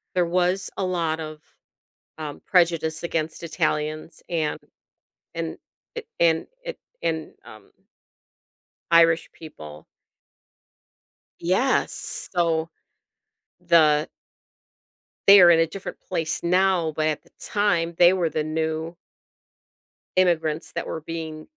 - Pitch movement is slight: Yes, narrow, 2.0 semitones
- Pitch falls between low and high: Yes, medium, 165 Hz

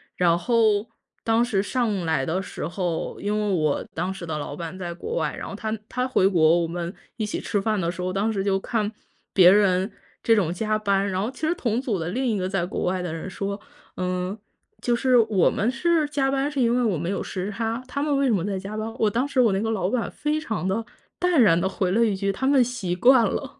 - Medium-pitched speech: No, high, 205 Hz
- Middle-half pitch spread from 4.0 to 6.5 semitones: Yes, average, 4.4 semitones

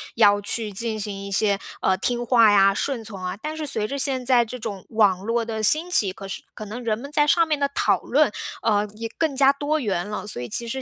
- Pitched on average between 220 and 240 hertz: Yes, high, 225 Hz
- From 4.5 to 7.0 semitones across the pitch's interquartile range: Yes, average, 4.8 semitones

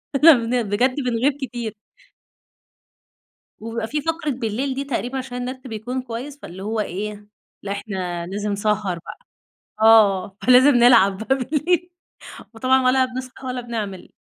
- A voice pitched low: No, high, 240 Hz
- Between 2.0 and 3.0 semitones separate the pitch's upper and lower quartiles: No, average, 3.7 semitones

